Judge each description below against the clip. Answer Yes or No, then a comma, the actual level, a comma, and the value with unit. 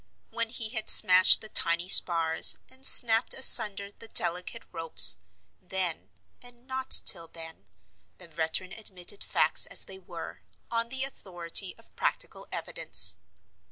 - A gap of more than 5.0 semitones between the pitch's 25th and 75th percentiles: Yes, wide, 5.4 semitones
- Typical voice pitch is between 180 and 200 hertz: Yes, high, 190 Hz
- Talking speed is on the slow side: Yes, slow, 130 wpm